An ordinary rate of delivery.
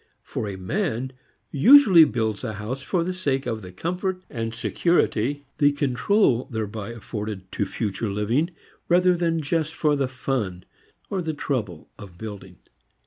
Yes: average, 150 wpm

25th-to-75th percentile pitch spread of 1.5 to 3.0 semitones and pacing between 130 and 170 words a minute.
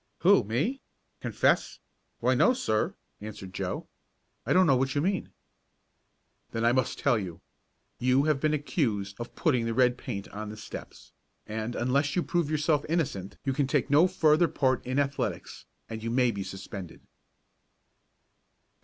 No: wide, 5.5 semitones; average, 160 wpm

